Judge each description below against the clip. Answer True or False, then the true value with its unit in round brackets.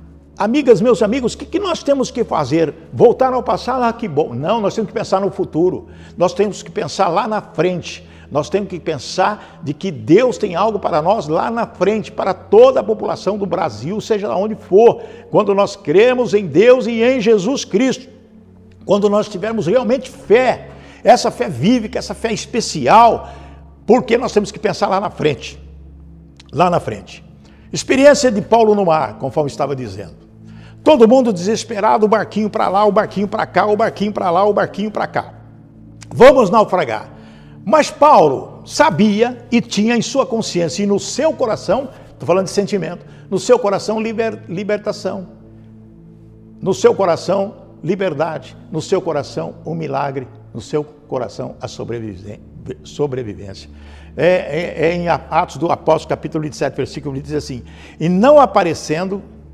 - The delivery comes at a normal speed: True (170 wpm)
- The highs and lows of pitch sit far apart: True (7.0 semitones)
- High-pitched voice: True (195 Hz)